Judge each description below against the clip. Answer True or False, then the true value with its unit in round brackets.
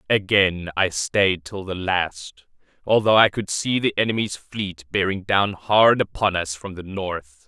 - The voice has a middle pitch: False (95 Hz)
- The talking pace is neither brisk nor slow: True (170 wpm)